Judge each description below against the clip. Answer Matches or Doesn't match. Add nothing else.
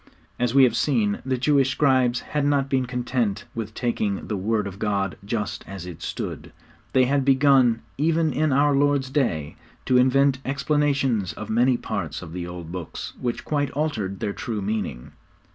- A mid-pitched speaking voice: Doesn't match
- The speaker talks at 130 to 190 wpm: Matches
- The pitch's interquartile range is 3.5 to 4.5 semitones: Doesn't match